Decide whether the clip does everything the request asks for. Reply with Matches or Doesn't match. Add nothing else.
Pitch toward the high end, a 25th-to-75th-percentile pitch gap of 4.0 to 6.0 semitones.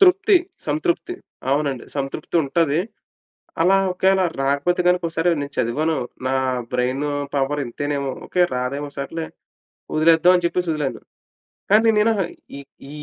Doesn't match